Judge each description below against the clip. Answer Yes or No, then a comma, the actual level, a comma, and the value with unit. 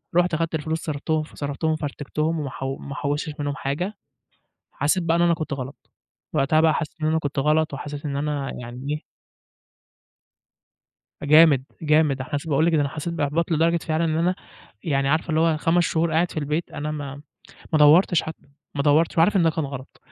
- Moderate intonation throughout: No, narrow, 2.3 semitones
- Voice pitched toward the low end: No, medium, 155 Hz